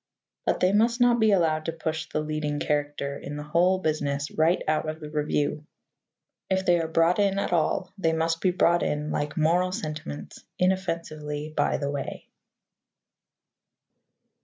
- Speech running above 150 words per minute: Yes, average, 160 wpm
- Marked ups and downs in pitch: No, average, 3.3 semitones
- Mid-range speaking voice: Yes, medium, 160 Hz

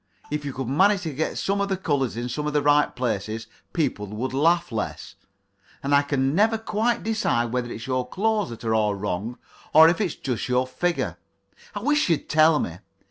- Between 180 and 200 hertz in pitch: No, medium, 140 Hz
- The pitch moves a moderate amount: No, wide, 6.6 semitones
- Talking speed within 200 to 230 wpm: Yes, fast, 205 wpm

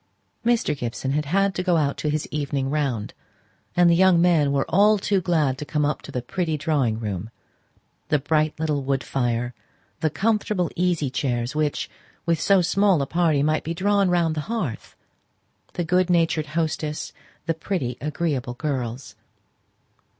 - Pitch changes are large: No, average, 4.2 semitones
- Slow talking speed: No, average, 165 wpm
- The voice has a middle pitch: Yes, medium, 155 Hz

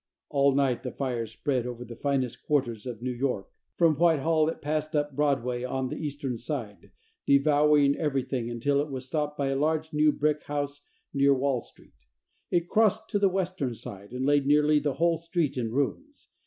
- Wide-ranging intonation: No, average, 3.2 semitones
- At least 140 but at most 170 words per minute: No, average, 185 wpm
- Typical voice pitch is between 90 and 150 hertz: Yes, medium, 140 Hz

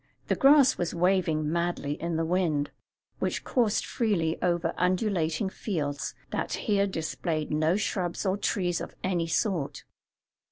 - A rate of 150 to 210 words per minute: No, slow, 135 wpm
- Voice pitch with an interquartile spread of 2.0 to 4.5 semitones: Yes, average, 3.3 semitones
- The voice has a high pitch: No, medium, 175 Hz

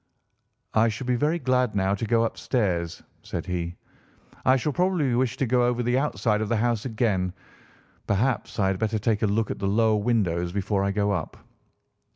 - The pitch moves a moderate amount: Yes, average, 3.9 semitones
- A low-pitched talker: Yes, low, 110 Hz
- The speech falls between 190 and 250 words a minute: Yes, average, 195 wpm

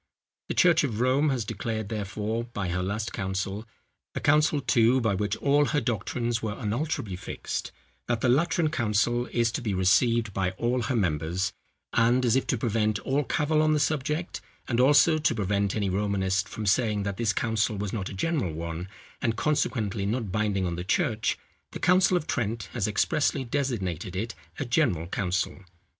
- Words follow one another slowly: No, average, 175 wpm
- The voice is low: Yes, low, 115 Hz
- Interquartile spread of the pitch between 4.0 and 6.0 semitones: Yes, average, 4.6 semitones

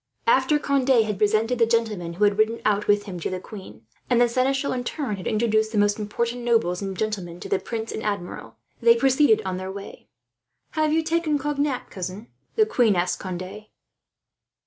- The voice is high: Yes, high, 220 Hz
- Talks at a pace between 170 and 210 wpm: Yes, average, 190 wpm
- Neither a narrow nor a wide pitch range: Yes, average, 4.3 semitones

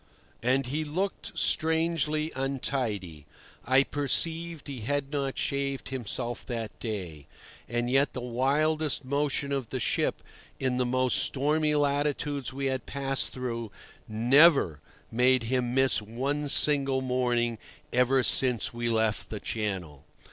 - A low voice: Yes, low, 130 Hz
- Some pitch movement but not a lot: Yes, average, 3.2 semitones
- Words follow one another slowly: Yes, slow, 130 wpm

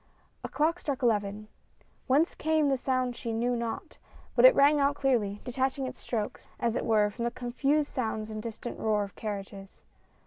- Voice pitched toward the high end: Yes, high, 240 Hz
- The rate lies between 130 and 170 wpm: No, average, 180 wpm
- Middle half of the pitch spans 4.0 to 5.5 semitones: Yes, average, 4.3 semitones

